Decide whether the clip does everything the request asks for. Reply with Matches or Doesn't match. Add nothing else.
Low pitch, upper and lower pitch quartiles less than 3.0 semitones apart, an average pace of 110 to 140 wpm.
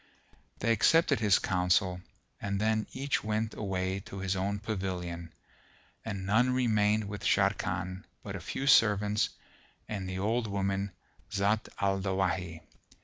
Matches